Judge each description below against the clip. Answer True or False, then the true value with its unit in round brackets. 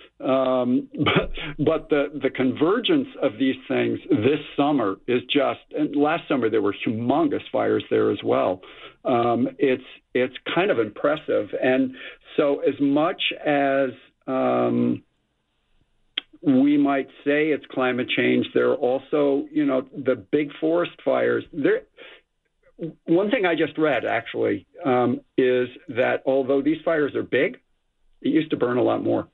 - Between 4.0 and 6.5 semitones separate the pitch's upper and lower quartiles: True (4.6 semitones)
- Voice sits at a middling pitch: True (145 Hz)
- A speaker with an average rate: True (145 wpm)